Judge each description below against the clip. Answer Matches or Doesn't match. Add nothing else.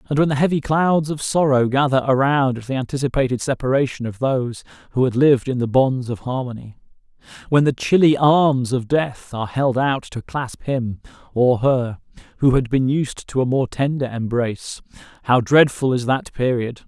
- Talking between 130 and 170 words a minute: Doesn't match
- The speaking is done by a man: Matches